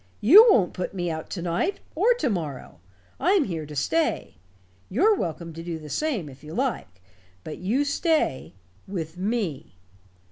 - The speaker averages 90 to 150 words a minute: No, average, 165 wpm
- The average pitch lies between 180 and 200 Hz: Yes, medium, 185 Hz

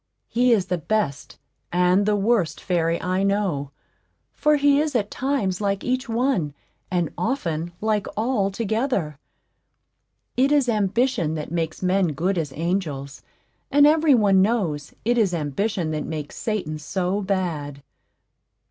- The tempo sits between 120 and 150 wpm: Yes, average, 140 wpm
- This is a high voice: Yes, high, 195 Hz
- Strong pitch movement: Yes, wide, 5.9 semitones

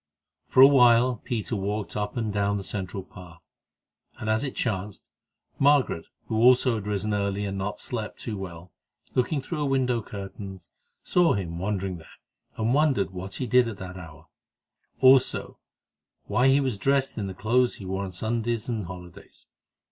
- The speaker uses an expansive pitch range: No, average, 4.5 semitones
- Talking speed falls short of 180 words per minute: Yes, average, 170 wpm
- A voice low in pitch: Yes, low, 105 Hz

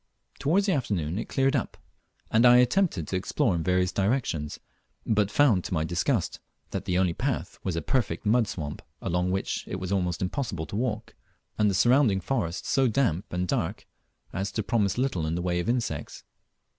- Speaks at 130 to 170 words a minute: No, average, 190 wpm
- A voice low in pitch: Yes, low, 100 Hz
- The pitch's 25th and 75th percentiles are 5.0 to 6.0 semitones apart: Yes, wide, 5.5 semitones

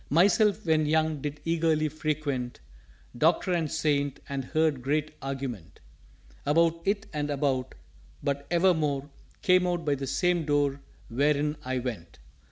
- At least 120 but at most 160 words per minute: Yes, average, 140 wpm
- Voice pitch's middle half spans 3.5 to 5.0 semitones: No, average, 2.9 semitones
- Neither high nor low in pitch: Yes, medium, 150 Hz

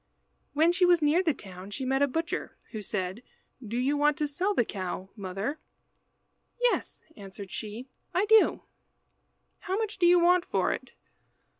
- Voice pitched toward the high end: Yes, very high, 285 Hz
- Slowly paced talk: No, average, 165 wpm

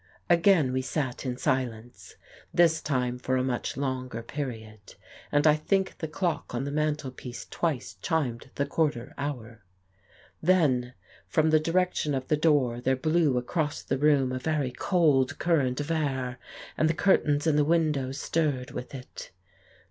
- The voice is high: No, medium, 140 Hz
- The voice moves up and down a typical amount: Yes, average, 3.6 semitones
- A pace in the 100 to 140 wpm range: No, average, 165 wpm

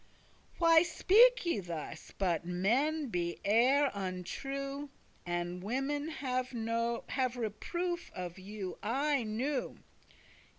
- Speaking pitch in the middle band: No, high, 245 Hz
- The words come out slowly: Yes, slow, 95 wpm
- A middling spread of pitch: No, wide, 7.3 semitones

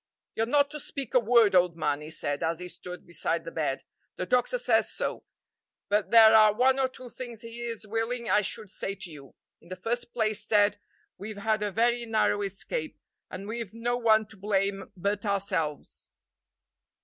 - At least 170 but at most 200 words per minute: Yes, average, 190 wpm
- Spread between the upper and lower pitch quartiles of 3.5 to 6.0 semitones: Yes, average, 3.8 semitones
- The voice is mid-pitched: No, high, 210 Hz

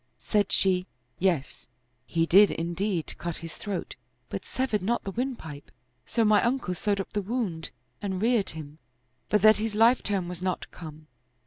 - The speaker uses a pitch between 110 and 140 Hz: No, high, 195 Hz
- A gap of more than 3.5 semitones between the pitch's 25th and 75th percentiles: Yes, average, 4.3 semitones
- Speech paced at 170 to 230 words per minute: Yes, average, 175 wpm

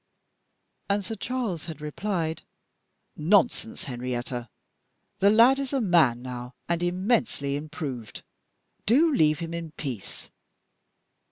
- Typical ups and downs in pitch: No, wide, 7.1 semitones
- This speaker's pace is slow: Yes, slow, 110 wpm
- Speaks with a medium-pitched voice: Yes, medium, 165 Hz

